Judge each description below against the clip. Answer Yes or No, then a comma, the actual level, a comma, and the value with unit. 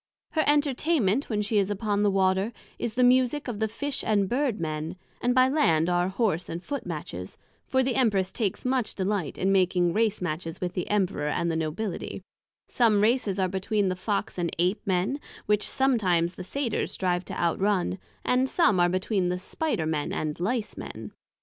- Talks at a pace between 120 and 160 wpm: No, average, 185 wpm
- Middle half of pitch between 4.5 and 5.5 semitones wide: Yes, average, 5.1 semitones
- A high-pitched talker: Yes, high, 200 Hz